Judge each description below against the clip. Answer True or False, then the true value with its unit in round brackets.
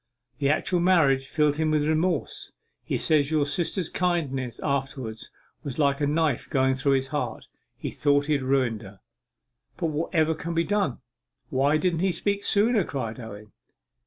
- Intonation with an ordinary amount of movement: True (3.8 semitones)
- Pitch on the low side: False (145 Hz)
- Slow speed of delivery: False (165 wpm)